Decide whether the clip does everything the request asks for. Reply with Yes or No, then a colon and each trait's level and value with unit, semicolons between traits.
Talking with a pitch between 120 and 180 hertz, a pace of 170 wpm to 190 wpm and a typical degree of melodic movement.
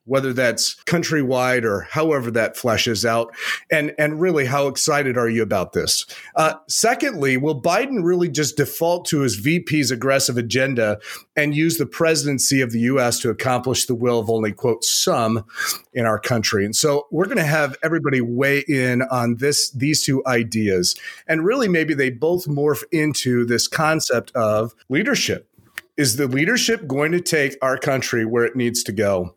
Yes: low, 135 Hz; average, 175 wpm; average, 4.3 semitones